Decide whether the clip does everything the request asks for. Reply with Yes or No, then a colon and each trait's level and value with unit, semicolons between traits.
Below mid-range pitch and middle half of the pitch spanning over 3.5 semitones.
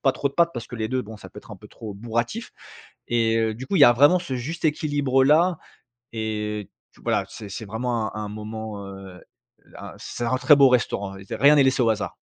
Yes: low, 120 Hz; average, 4.4 semitones